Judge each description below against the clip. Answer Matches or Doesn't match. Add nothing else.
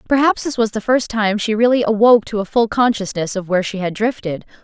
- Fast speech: Matches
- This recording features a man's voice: Doesn't match